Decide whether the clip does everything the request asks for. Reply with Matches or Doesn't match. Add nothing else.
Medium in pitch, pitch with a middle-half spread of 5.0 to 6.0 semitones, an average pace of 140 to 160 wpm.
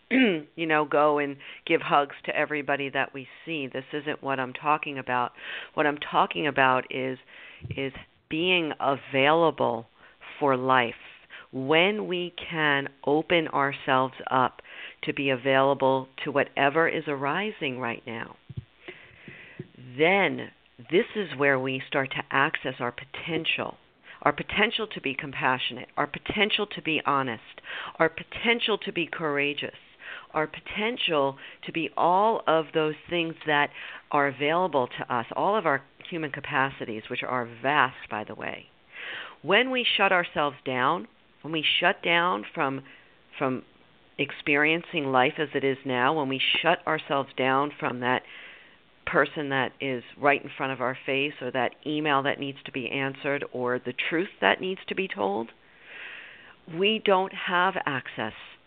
Doesn't match